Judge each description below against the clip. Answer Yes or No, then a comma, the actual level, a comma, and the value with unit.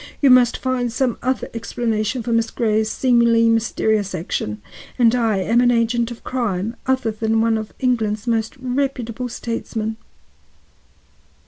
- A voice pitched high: Yes, high, 230 Hz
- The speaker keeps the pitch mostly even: Yes, narrow, 1.9 semitones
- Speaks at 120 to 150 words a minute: Yes, slow, 135 wpm